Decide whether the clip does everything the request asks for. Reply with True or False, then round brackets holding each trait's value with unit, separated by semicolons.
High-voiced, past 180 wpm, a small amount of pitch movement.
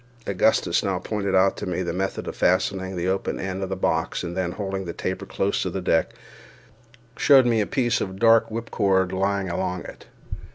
False (95 Hz; 200 wpm; 1.5 semitones)